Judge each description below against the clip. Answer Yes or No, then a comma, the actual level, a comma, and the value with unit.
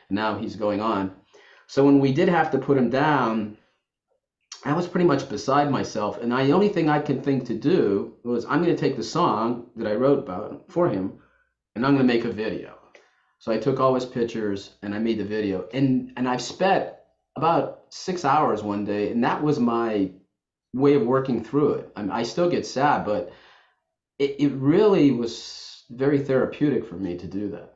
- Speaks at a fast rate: Yes, fast, 210 wpm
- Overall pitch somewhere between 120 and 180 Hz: Yes, low, 125 Hz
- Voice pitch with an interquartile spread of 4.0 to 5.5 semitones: Yes, average, 4.7 semitones